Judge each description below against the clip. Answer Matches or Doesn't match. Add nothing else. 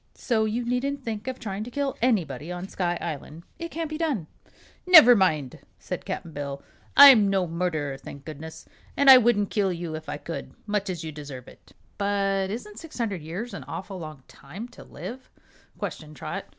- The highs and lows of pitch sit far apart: Matches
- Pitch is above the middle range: Matches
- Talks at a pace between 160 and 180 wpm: Doesn't match